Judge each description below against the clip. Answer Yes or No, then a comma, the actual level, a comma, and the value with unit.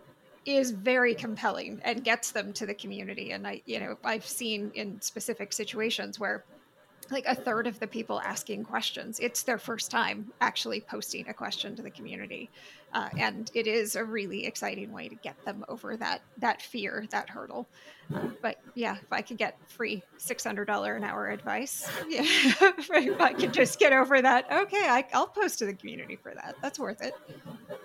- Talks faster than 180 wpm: Yes, average, 190 wpm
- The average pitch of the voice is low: No, high, 230 Hz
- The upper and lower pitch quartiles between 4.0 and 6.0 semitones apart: No, average, 3.1 semitones